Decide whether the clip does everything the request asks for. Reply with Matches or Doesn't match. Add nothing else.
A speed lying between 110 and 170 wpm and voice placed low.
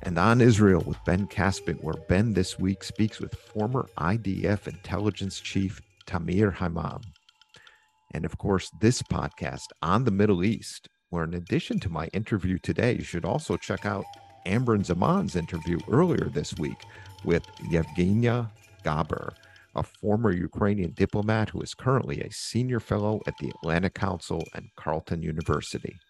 Matches